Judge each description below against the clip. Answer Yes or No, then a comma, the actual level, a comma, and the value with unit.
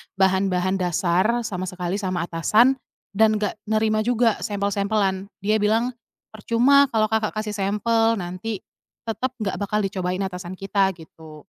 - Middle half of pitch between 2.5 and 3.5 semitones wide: Yes, average, 2.8 semitones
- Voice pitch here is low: No, high, 200 Hz